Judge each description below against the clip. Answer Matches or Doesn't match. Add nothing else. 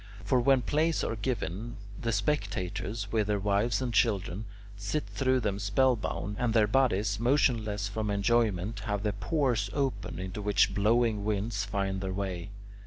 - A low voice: Matches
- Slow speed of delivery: Doesn't match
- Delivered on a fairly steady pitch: Doesn't match